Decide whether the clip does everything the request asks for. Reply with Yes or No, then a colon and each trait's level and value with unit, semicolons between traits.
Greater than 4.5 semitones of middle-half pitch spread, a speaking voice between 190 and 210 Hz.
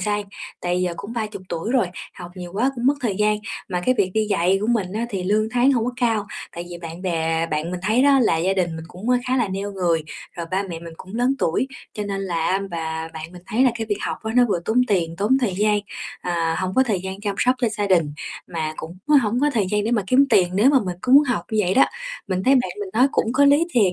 Yes: average, 5.1 semitones; high, 200 Hz